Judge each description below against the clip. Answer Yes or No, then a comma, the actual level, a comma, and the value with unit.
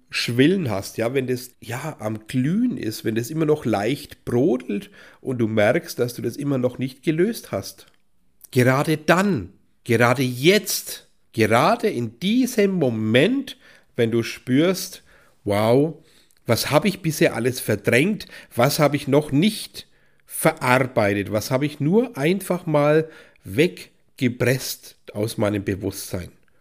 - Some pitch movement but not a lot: No, wide, 5.8 semitones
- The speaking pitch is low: Yes, low, 130 Hz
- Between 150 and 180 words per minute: No, average, 135 wpm